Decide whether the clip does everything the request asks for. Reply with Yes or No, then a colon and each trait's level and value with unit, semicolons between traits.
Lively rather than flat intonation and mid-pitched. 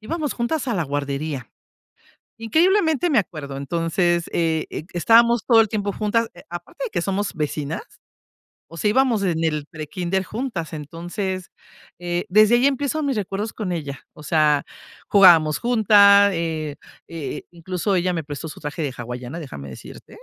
Yes: wide, 5.9 semitones; medium, 175 Hz